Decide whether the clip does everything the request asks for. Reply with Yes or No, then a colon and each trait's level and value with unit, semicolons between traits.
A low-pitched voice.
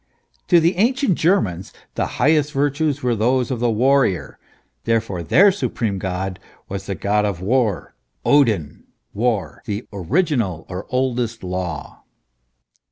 Yes: low, 115 Hz